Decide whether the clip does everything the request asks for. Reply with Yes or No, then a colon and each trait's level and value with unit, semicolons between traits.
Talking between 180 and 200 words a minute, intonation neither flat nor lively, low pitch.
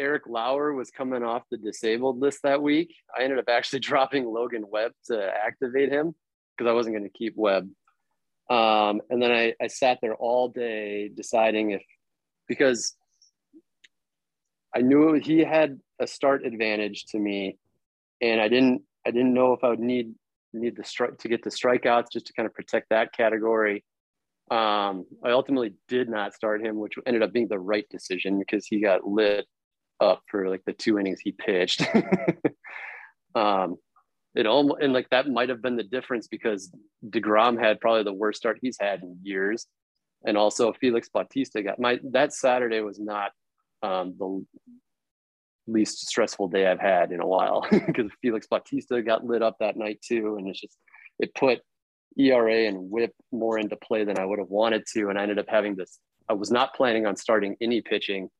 Yes: average, 185 wpm; average, 3.3 semitones; low, 115 Hz